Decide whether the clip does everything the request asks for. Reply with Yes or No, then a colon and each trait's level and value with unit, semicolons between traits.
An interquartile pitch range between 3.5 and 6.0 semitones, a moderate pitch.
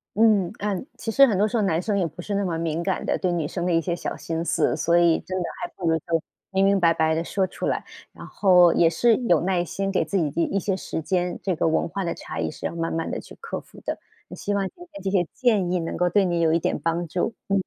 No: average, 2.9 semitones; medium, 180 Hz